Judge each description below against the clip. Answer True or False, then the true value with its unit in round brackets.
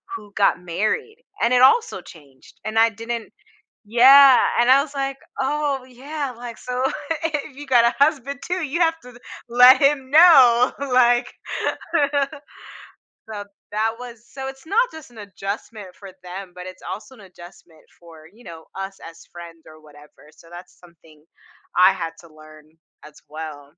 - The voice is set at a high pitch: True (235 Hz)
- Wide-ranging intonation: True (7.2 semitones)